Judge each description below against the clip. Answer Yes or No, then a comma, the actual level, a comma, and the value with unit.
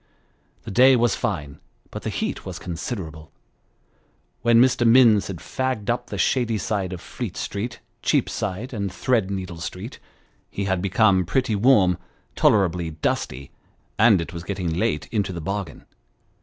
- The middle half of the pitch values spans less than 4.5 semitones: No, average, 4.8 semitones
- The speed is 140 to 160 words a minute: Yes, average, 150 wpm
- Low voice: Yes, low, 100 Hz